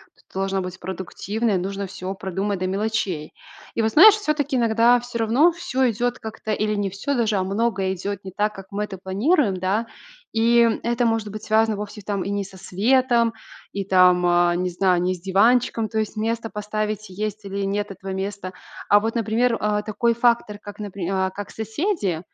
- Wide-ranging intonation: No, average, 3.1 semitones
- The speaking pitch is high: Yes, high, 210 Hz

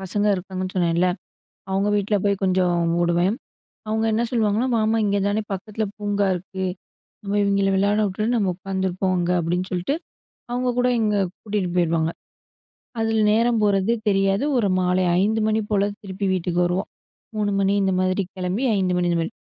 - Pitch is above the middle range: Yes, high, 195 Hz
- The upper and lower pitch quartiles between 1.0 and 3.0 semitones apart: Yes, narrow, 2.5 semitones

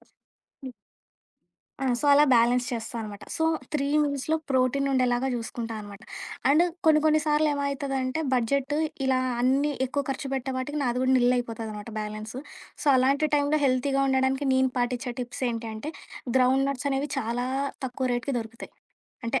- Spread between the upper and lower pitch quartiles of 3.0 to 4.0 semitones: No, narrow, 2.5 semitones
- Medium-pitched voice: No, very high, 260 Hz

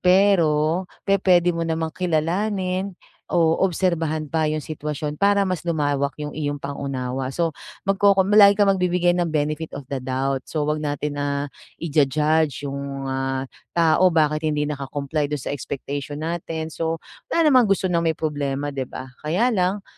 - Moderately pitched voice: Yes, medium, 155 Hz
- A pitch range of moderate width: Yes, average, 3.9 semitones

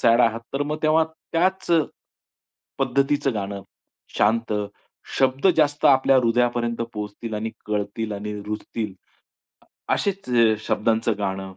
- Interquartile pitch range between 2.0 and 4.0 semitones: No, average, 4.8 semitones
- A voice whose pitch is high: No, low, 115 Hz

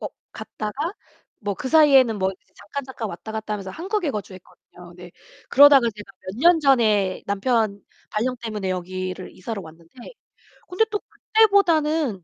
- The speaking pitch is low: No, high, 220 Hz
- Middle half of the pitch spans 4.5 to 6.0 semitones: No, wide, 7.0 semitones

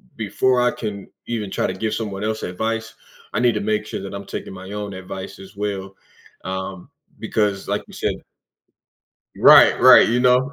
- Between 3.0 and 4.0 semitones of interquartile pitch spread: No, narrow, 2.6 semitones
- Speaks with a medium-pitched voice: No, low, 105 Hz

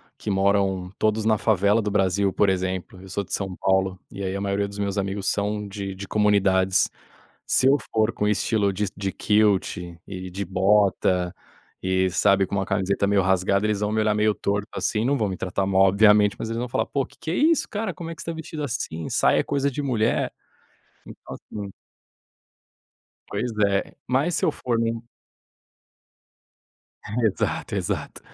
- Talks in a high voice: No, low, 100 Hz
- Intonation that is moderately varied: No, narrow, 2.3 semitones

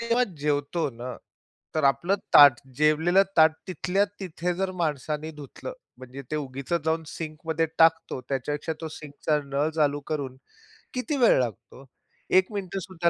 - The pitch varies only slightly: No, average, 3.5 semitones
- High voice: No, medium, 155 Hz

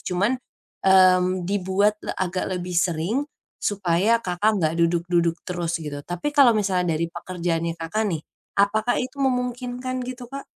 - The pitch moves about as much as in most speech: Yes, average, 4.4 semitones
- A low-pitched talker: No, medium, 185 Hz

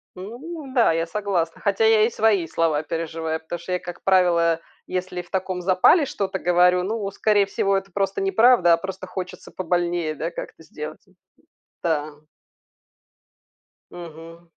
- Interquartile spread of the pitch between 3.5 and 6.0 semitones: No, average, 2.9 semitones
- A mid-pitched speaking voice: Yes, medium, 180 Hz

